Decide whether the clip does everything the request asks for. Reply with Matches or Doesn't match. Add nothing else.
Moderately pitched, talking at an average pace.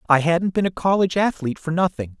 Doesn't match